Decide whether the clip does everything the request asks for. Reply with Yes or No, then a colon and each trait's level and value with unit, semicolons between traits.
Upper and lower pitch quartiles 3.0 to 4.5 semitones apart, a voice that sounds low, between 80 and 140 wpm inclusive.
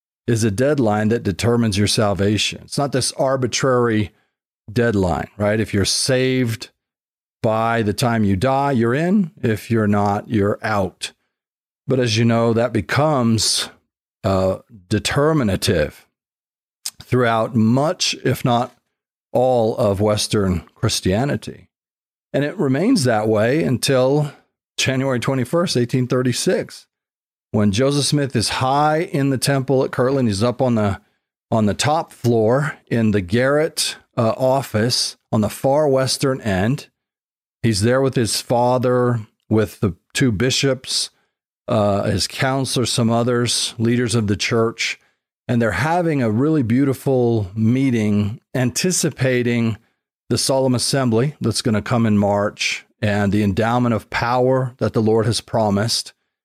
Yes: average, 3.4 semitones; low, 120 Hz; slow, 135 wpm